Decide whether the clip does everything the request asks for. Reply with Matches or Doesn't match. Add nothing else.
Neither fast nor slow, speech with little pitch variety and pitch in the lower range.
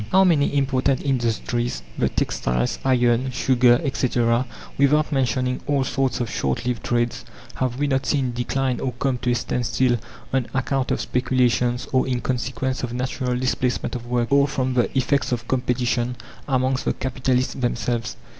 Matches